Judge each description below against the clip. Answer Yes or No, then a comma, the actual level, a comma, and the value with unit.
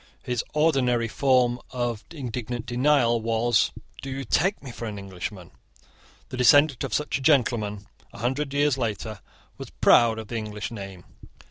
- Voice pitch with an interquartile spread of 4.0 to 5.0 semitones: No, average, 3.5 semitones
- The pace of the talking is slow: No, average, 155 wpm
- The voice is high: No, low, 120 Hz